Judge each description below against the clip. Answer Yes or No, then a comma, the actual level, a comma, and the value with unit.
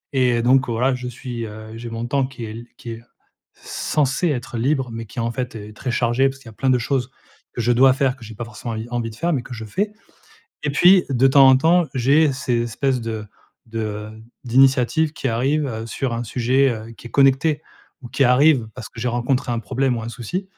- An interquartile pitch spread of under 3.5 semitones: Yes, average, 2.8 semitones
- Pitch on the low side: Yes, low, 125 Hz